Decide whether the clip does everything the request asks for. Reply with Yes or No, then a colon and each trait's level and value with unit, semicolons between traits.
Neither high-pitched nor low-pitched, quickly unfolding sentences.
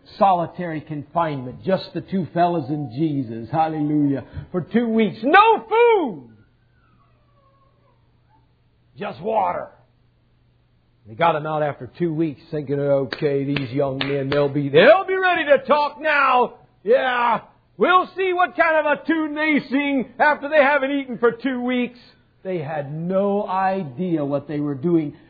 No: medium, 175 Hz; average, 145 wpm